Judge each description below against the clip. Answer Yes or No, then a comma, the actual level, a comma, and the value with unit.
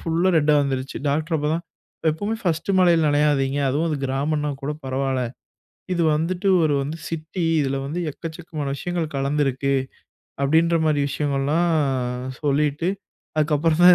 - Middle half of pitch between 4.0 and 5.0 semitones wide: No, average, 3.0 semitones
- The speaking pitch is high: No, medium, 150 Hz